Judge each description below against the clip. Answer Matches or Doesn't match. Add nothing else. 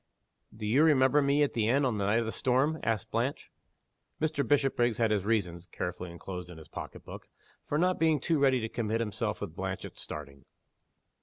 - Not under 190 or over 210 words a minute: Matches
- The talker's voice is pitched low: Matches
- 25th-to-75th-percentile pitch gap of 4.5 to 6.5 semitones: Matches